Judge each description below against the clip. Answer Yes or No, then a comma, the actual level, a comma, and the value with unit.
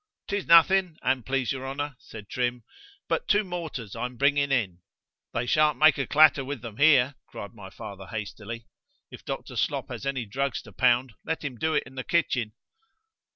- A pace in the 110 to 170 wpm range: No, average, 180 wpm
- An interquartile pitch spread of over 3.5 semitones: Yes, average, 4.1 semitones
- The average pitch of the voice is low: Yes, low, 130 Hz